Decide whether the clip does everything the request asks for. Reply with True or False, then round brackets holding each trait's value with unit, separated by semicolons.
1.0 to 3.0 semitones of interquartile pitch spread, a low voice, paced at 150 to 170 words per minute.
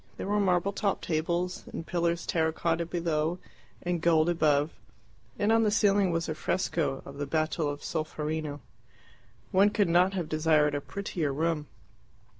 False (2.7 semitones; 165 Hz; 160 wpm)